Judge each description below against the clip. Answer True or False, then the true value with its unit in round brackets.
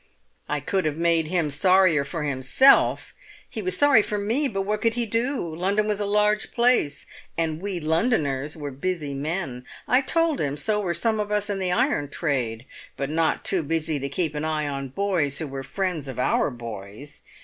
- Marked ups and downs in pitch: True (6.2 semitones)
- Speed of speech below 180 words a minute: False (195 wpm)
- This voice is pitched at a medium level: True (165 Hz)